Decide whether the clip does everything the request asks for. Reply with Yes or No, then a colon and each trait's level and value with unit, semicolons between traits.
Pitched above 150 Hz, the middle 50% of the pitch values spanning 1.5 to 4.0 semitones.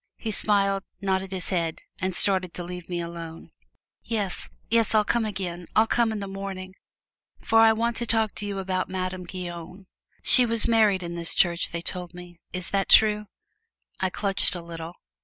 Yes: high, 190 Hz; average, 3.1 semitones